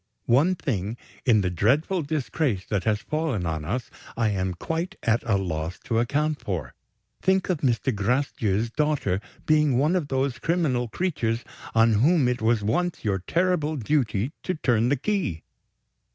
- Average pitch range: No, wide, 6.6 semitones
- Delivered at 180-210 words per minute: No, average, 160 wpm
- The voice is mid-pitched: No, low, 125 Hz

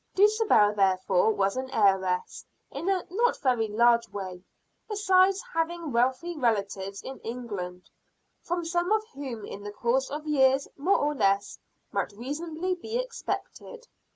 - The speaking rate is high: No, average, 140 wpm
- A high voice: Yes, very high, 265 Hz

